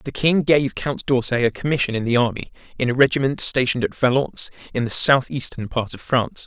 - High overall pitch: No, low, 130 Hz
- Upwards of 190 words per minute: Yes, fast, 205 wpm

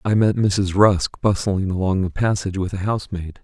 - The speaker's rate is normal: Yes, average, 190 wpm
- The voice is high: No, very low, 95 Hz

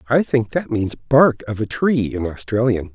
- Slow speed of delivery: No, fast, 205 wpm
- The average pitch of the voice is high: No, low, 115 Hz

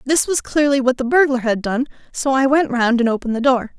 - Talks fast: Yes, fast, 255 wpm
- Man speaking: No, female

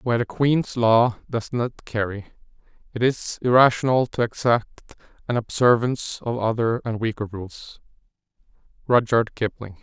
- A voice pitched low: Yes, low, 115 Hz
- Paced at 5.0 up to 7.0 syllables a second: No, 4.8 syllables/s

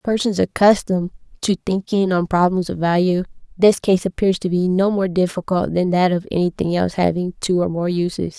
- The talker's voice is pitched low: No, medium, 185 Hz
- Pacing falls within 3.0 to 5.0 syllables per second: No, 5.5 syllables/s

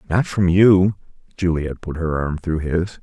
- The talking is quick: No, average, 180 wpm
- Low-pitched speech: Yes, very low, 90 Hz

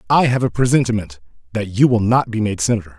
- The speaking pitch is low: Yes, low, 110 Hz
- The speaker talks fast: Yes, fast, 220 wpm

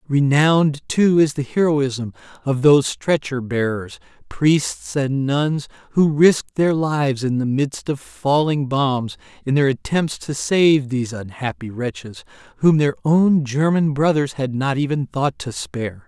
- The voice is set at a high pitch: No, medium, 140 Hz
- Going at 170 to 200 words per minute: No, average, 155 wpm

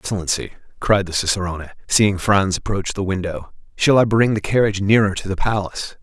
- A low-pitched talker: Yes, low, 100 Hz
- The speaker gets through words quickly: No, average, 180 wpm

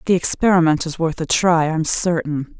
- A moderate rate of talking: Yes, average, 185 wpm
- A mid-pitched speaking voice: Yes, medium, 165 Hz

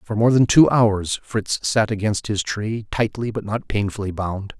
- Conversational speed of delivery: Yes, average, 195 wpm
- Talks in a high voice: No, low, 105 Hz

